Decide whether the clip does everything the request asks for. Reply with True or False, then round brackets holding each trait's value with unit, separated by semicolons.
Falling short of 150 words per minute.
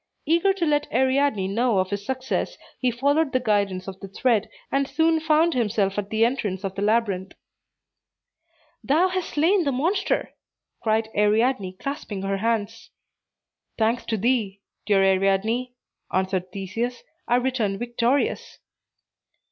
True (140 wpm)